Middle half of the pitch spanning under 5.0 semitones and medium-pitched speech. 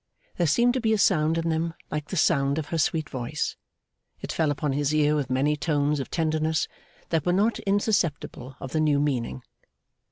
Yes: narrow, 2.4 semitones; medium, 155 Hz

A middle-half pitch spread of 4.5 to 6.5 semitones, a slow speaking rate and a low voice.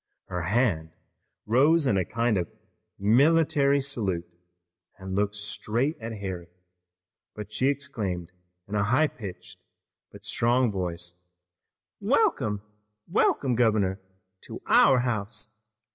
Yes: average, 5.1 semitones; slow, 110 wpm; low, 105 Hz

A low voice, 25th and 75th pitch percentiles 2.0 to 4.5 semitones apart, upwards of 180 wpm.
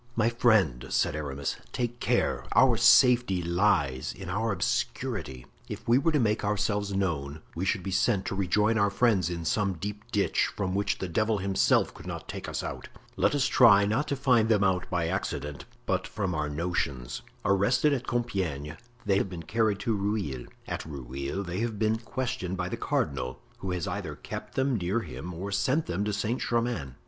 No: low, 100 Hz; average, 4.9 semitones; average, 190 wpm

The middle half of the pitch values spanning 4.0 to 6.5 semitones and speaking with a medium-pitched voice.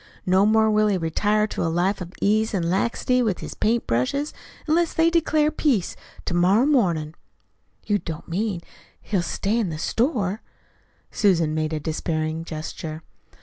No: average, 5.2 semitones; high, 195 Hz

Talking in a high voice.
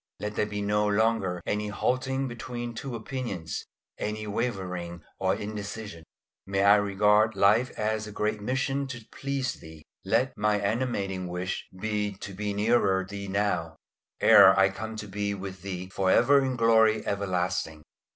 No: low, 105 Hz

